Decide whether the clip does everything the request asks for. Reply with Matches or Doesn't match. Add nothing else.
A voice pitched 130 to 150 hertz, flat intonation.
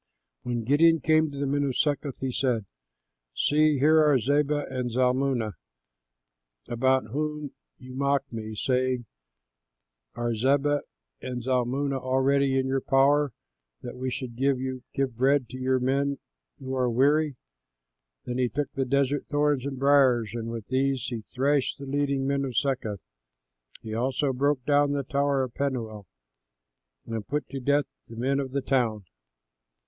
Matches